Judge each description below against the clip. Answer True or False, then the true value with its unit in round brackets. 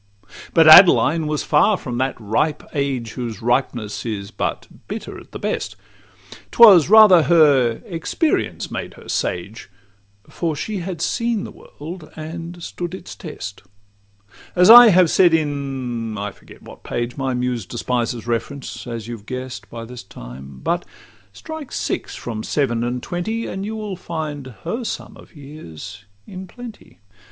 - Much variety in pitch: True (6.9 semitones)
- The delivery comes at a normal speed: True (150 wpm)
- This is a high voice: False (140 Hz)